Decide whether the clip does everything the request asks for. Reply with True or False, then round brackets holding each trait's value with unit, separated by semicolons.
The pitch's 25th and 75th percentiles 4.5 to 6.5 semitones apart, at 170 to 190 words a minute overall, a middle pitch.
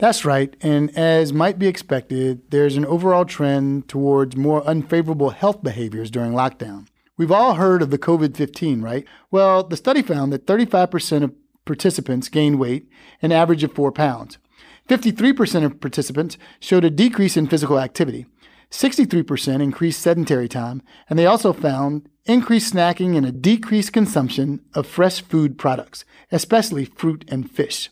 False (5.2 semitones; 155 wpm; 155 Hz)